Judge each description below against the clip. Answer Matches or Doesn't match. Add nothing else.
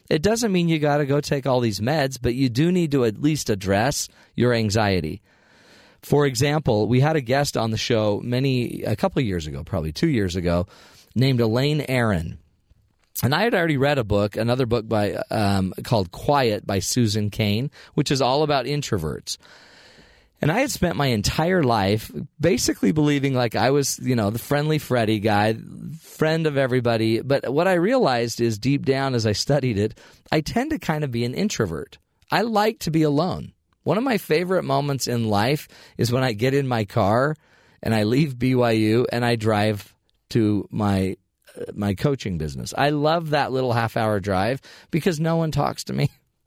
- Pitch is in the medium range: Doesn't match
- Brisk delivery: Doesn't match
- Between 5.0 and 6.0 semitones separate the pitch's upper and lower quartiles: Matches